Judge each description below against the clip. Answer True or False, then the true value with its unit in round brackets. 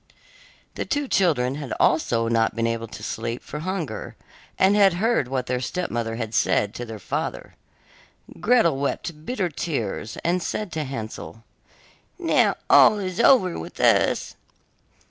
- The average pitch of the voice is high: False (145 Hz)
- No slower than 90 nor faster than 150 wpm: True (145 wpm)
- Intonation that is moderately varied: False (8.1 semitones)